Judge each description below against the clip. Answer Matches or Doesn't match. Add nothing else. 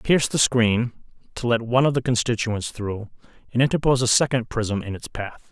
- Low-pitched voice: Matches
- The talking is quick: Doesn't match